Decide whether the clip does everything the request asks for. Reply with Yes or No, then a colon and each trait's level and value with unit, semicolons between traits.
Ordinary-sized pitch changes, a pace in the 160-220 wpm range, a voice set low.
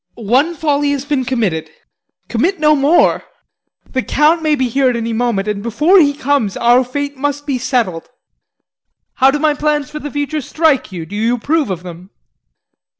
No: average, 4.2 semitones; average, 180 wpm; very high, 270 Hz